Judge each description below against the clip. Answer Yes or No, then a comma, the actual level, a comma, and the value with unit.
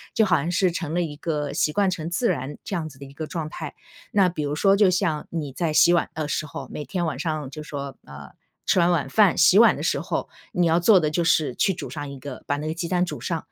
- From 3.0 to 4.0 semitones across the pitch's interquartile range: Yes, average, 3.4 semitones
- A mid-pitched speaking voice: Yes, medium, 160 Hz